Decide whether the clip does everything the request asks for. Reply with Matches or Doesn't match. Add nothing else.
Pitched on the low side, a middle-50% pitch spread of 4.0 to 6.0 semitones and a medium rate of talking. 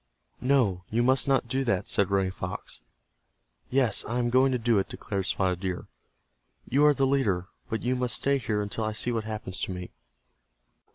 Matches